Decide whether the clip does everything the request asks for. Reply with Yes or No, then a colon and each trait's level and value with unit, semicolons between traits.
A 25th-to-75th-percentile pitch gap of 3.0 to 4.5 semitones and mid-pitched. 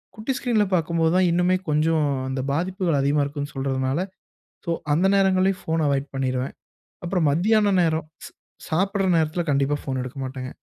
No: average, 4.9 semitones; medium, 160 Hz